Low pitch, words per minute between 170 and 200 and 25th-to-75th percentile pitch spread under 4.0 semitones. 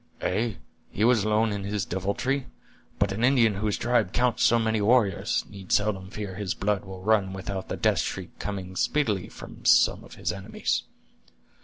Yes: low, 105 Hz; average, 175 wpm; average, 2.8 semitones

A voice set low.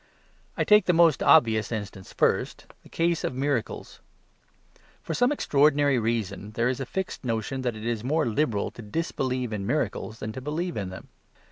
Yes: low, 125 Hz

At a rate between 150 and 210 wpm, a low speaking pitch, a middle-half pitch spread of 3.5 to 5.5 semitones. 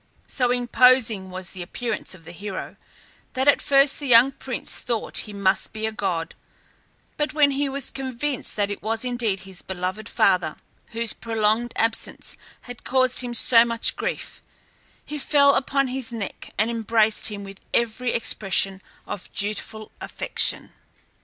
No: average, 155 wpm; high, 230 Hz; average, 4.0 semitones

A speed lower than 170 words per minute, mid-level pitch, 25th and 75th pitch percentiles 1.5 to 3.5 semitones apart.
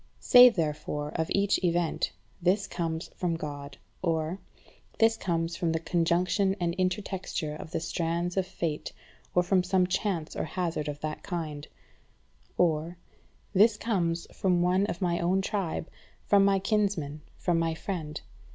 Yes: average, 150 wpm; medium, 175 Hz; average, 2.8 semitones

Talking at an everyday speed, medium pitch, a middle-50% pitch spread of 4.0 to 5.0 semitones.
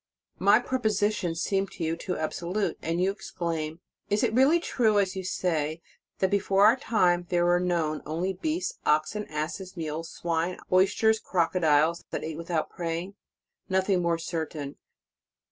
No: average, 155 wpm; medium, 180 Hz; average, 3.3 semitones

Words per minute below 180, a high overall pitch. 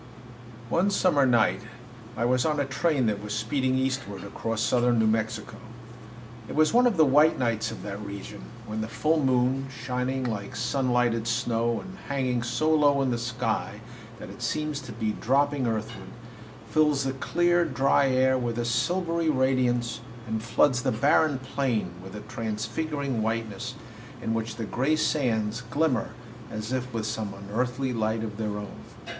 No: average, 170 wpm; low, 125 Hz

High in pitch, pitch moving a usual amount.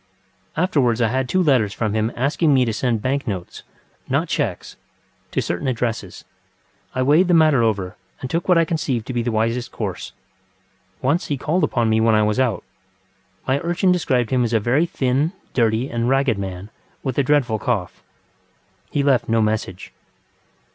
No: low, 125 Hz; average, 4.3 semitones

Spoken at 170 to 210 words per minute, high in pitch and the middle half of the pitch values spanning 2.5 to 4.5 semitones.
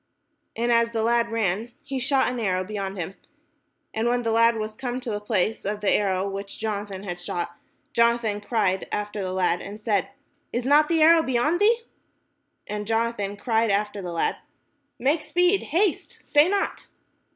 Yes: average, 180 wpm; high, 225 Hz; average, 3.5 semitones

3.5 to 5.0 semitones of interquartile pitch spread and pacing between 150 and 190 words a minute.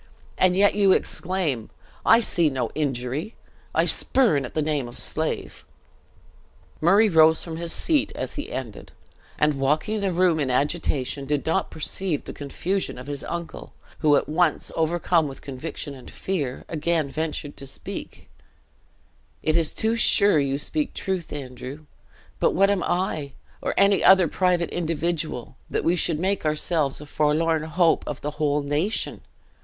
Yes: average, 4.0 semitones; average, 160 wpm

